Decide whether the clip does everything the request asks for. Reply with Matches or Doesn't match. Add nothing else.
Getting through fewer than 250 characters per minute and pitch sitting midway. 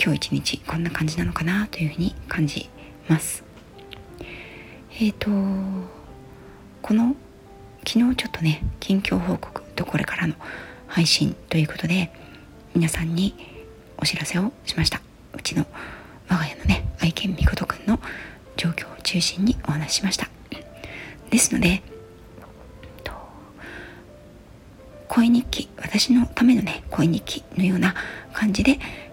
Matches